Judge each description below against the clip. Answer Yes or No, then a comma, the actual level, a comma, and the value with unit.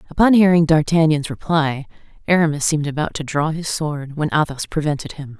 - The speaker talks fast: No, average, 165 wpm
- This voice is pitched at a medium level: Yes, medium, 155 Hz